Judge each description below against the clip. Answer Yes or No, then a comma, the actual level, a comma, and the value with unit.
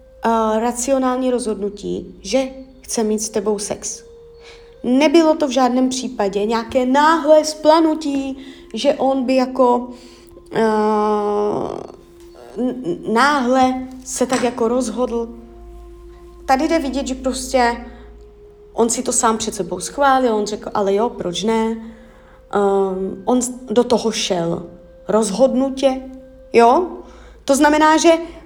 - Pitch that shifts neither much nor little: Yes, average, 3.9 semitones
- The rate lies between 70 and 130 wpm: Yes, average, 120 wpm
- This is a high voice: Yes, very high, 250 Hz